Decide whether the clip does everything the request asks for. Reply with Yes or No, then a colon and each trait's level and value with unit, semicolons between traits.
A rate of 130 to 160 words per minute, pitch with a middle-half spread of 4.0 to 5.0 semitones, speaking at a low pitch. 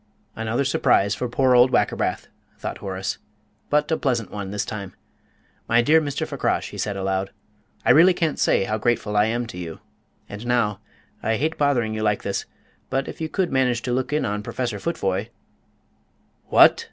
No: average, 185 wpm; average, 4.5 semitones; low, 115 Hz